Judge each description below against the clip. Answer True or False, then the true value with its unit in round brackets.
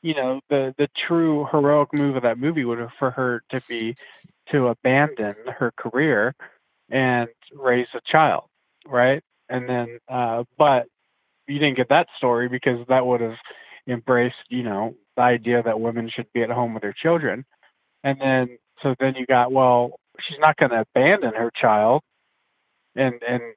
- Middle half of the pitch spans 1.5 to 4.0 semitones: True (2.4 semitones)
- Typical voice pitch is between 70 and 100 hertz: False (125 Hz)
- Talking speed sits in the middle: True (175 wpm)